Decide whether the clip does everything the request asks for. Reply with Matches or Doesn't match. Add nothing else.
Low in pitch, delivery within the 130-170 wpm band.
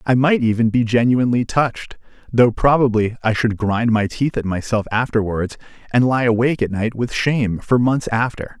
Doesn't match